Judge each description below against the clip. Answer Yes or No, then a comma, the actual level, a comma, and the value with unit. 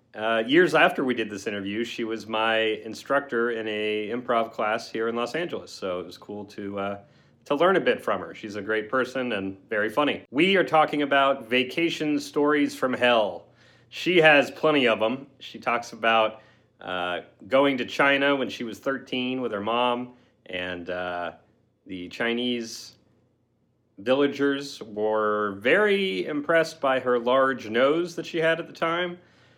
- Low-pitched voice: Yes, low, 120 Hz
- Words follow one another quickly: No, average, 170 wpm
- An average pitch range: Yes, average, 4.6 semitones